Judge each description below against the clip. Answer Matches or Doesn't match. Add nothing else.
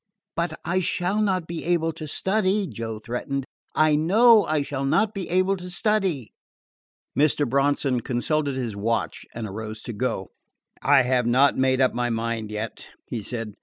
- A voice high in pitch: Doesn't match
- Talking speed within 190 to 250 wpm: Doesn't match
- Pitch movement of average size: Doesn't match